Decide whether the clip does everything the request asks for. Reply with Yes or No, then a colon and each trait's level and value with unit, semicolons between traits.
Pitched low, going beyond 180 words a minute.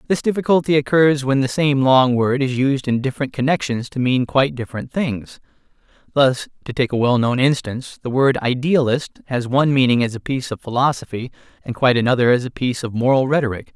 Yes: low, 130 Hz; average, 190 wpm